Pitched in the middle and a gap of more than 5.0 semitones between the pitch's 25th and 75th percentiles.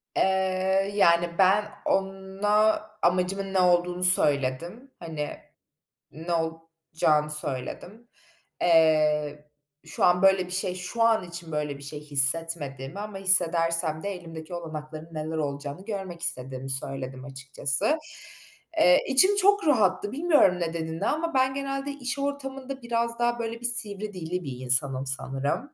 Yes: medium, 175 Hz; wide, 5.5 semitones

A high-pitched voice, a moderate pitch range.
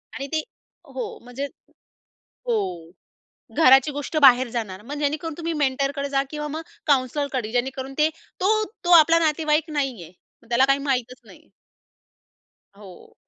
Yes: very high, 275 Hz; average, 3.3 semitones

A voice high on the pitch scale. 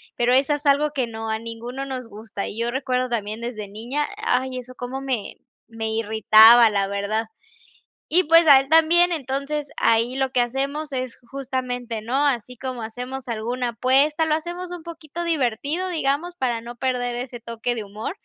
Yes: very high, 255 Hz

